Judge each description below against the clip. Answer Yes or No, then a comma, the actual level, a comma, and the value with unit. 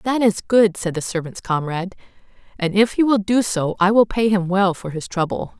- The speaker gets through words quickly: Yes, fast, 225 wpm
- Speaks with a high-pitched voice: Yes, high, 195 Hz